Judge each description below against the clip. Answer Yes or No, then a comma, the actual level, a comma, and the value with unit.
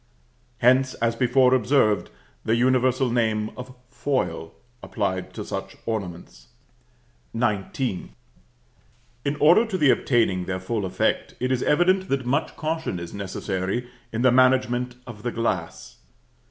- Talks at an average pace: No, slow, 130 wpm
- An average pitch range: Yes, average, 4.4 semitones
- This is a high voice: No, low, 120 Hz